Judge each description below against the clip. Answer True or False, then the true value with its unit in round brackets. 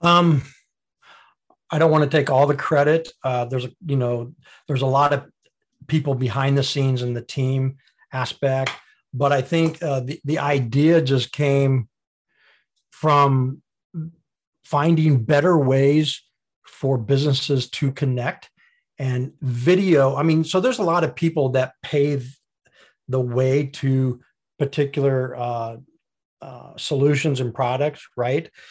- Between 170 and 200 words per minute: False (135 wpm)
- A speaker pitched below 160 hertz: True (140 Hz)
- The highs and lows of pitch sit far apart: False (2.8 semitones)